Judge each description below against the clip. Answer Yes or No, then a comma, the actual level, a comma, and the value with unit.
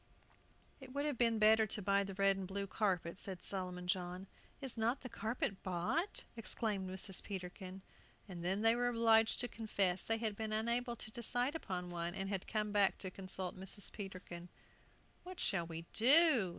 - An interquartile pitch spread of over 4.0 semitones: No, average, 3.5 semitones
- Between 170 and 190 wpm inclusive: Yes, average, 180 wpm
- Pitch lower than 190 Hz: No, high, 200 Hz